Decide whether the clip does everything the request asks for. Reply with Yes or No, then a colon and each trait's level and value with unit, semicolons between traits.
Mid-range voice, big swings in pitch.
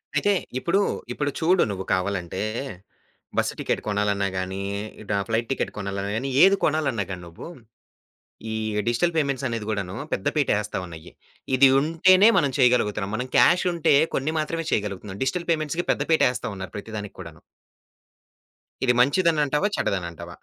No: low, 120 Hz; wide, 7.8 semitones